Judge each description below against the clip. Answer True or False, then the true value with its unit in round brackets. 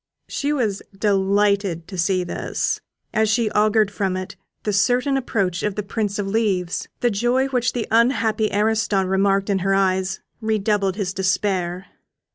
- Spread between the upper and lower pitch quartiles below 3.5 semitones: True (2.4 semitones)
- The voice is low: False (205 Hz)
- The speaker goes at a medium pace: True (155 wpm)